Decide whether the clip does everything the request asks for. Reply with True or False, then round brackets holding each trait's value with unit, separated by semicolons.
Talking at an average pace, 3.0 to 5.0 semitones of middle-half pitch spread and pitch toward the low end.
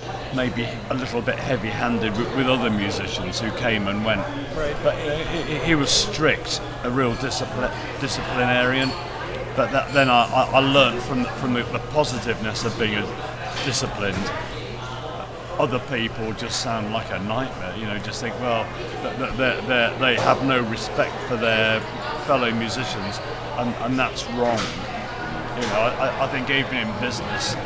False (150 wpm; 2.5 semitones; 125 Hz)